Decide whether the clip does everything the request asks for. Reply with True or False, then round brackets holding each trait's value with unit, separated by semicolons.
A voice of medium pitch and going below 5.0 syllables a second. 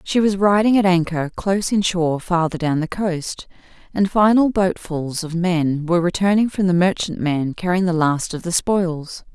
True (180 Hz; 4.7 syllables/s)